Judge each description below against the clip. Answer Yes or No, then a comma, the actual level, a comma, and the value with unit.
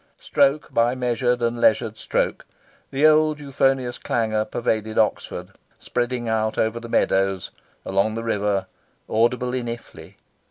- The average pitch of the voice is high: No, low, 115 Hz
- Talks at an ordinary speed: No, slow, 130 wpm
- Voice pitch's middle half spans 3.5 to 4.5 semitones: No, narrow, 2.4 semitones